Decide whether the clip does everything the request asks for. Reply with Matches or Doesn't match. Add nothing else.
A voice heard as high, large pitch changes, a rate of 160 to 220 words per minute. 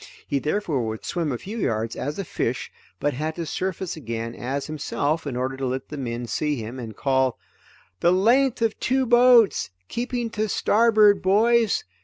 Doesn't match